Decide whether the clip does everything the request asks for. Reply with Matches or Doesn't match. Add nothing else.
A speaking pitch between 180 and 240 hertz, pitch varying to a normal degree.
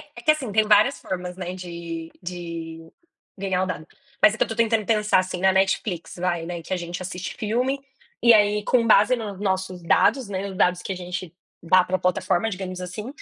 Matches